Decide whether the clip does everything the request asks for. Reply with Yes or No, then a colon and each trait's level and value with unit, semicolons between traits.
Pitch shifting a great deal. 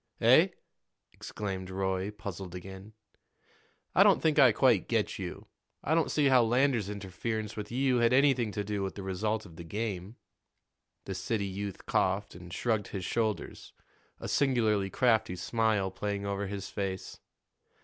No: average, 3.3 semitones